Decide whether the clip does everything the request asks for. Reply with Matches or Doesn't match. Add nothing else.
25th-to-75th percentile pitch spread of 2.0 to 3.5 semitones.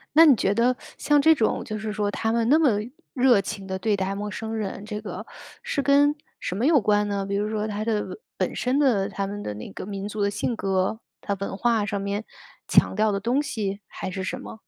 Matches